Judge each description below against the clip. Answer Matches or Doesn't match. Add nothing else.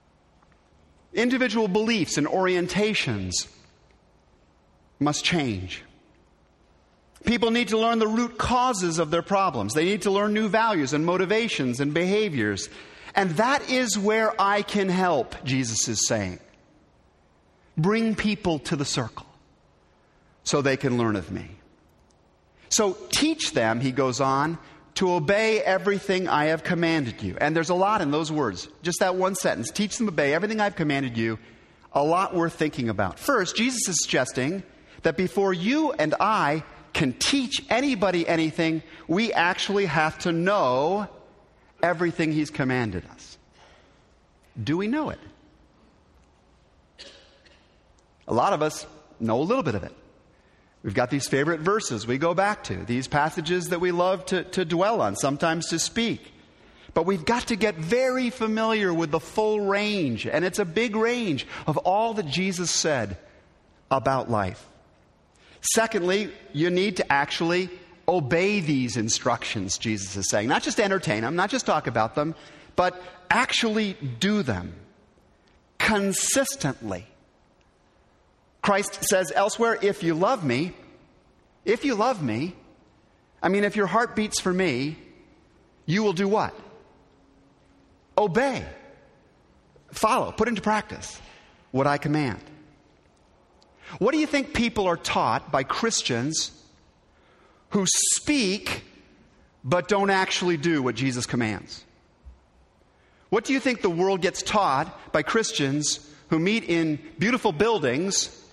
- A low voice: Doesn't match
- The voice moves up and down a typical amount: Doesn't match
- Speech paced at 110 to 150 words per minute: Matches